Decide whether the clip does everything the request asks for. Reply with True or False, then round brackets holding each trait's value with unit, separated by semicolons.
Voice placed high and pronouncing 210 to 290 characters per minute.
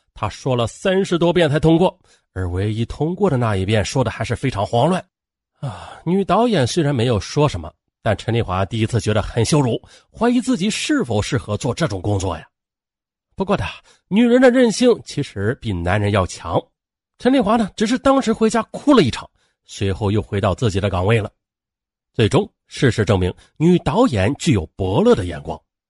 False (120 Hz; 280 characters per minute)